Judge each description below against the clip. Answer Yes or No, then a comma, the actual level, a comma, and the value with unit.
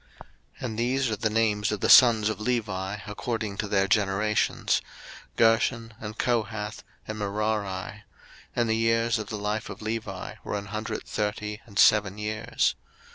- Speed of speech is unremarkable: Yes, average, 160 wpm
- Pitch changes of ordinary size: No, narrow, 1.5 semitones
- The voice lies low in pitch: Yes, low, 110 Hz